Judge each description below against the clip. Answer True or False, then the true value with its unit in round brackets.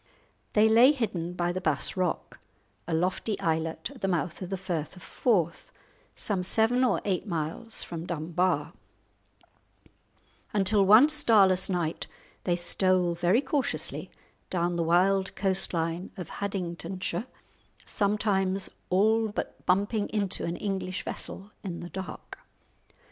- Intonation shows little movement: False (3.0 semitones)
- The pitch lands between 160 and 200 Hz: True (185 Hz)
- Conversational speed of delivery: False (130 wpm)